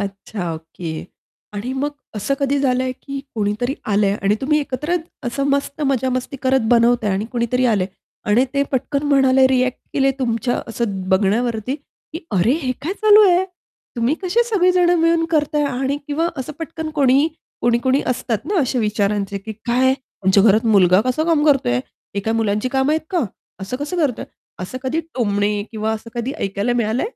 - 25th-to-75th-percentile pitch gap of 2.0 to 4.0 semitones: No, average, 4.9 semitones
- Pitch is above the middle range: Yes, very high, 255 Hz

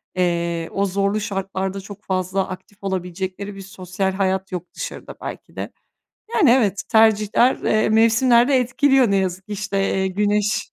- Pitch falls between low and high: No, high, 195 Hz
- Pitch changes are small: Yes, narrow, 2.2 semitones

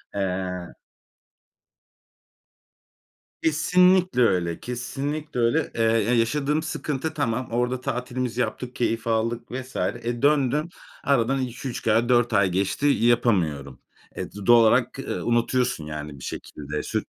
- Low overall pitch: Yes, low, 120 Hz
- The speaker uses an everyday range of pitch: Yes, average, 3.8 semitones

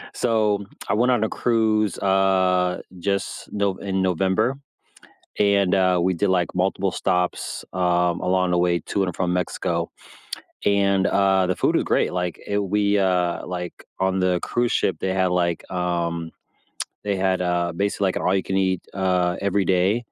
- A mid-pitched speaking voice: No, very low, 95 Hz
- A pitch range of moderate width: No, narrow, 1.9 semitones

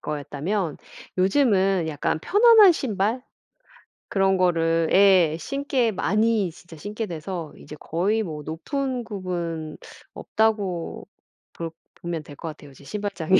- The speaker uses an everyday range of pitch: Yes, average, 4.8 semitones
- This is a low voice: No, medium, 185 Hz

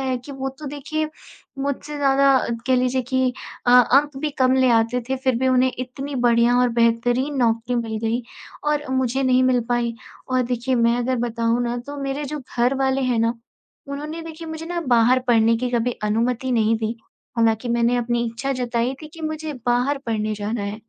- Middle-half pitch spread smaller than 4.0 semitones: Yes, narrow, 2.5 semitones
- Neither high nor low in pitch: No, very high, 250 Hz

